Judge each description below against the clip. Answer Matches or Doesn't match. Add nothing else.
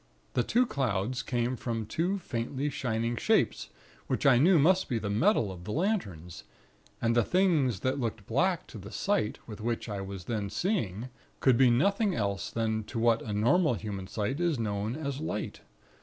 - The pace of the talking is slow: Doesn't match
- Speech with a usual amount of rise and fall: Doesn't match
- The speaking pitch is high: Doesn't match